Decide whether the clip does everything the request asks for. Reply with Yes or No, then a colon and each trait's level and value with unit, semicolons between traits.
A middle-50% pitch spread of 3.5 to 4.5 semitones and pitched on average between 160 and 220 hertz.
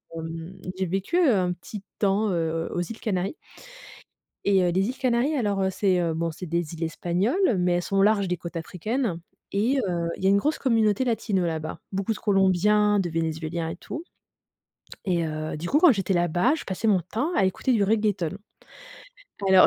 Yes: average, 3.8 semitones; high, 190 Hz